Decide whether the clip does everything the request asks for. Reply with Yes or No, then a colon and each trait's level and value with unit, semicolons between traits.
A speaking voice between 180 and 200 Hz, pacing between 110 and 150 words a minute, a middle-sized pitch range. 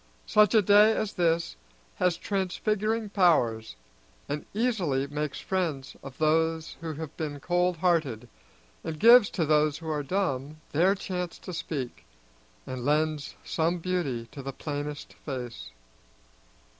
No: medium, 160 Hz; slow, 135 wpm; average, 4.2 semitones